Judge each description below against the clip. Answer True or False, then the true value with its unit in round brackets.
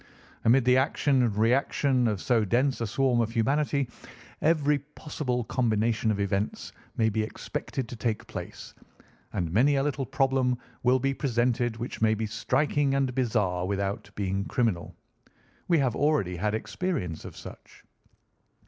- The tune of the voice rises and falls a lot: False (3.9 semitones)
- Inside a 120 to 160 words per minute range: True (150 wpm)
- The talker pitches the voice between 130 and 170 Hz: False (120 Hz)